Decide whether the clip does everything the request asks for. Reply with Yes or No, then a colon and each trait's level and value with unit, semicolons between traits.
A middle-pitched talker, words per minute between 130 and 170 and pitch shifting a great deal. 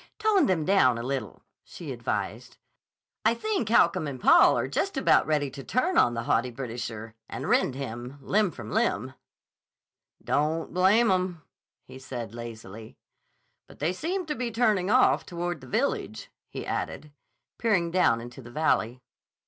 Yes: medium, 150 Hz; average, 155 wpm; wide, 8.6 semitones